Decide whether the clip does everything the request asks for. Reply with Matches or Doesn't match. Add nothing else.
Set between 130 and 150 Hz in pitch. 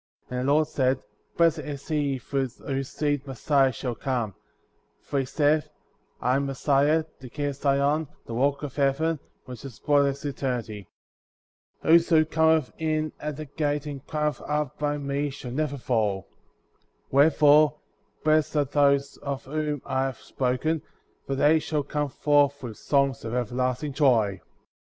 Matches